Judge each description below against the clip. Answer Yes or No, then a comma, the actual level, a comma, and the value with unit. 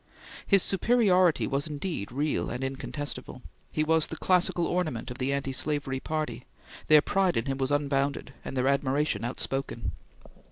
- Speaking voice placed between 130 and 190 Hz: Yes, medium, 140 Hz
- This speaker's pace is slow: No, average, 155 wpm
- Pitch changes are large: No, average, 3.2 semitones